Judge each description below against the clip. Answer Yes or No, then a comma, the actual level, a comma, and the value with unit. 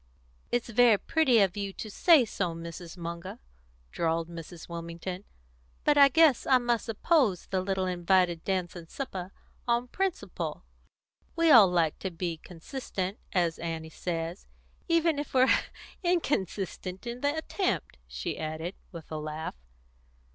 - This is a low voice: No, high, 190 Hz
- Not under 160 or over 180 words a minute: No, average, 140 wpm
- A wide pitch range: Yes, wide, 6.6 semitones